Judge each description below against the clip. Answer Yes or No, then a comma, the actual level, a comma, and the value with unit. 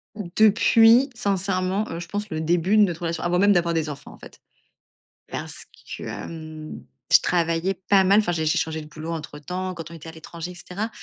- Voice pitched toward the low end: No, medium, 175 Hz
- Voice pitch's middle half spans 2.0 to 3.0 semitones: No, average, 3.5 semitones